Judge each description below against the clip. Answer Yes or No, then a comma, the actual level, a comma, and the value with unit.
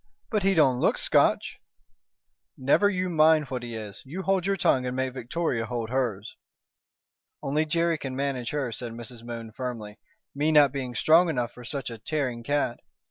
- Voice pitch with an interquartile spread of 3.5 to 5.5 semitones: Yes, average, 4.7 semitones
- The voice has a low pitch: Yes, low, 130 Hz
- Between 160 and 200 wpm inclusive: Yes, average, 180 wpm